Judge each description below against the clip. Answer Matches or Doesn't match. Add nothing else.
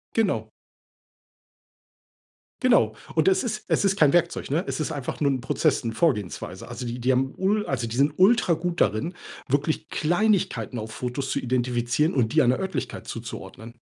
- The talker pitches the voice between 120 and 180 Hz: Matches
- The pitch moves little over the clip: Doesn't match